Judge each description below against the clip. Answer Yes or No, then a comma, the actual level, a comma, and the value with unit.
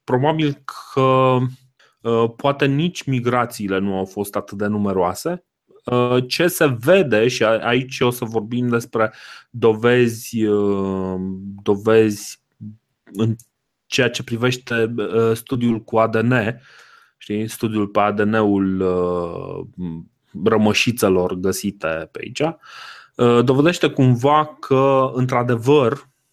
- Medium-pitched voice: No, low, 115 Hz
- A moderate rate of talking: No, slow, 105 wpm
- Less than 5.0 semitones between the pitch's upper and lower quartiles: Yes, average, 3.6 semitones